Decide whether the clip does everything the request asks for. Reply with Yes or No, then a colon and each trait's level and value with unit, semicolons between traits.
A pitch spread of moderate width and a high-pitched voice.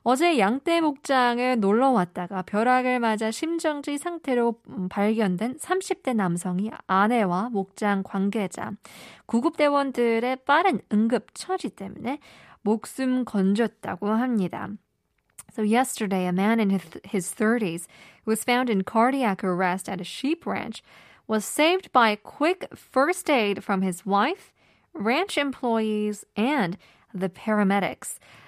Yes: average, 4.5 semitones; high, 220 Hz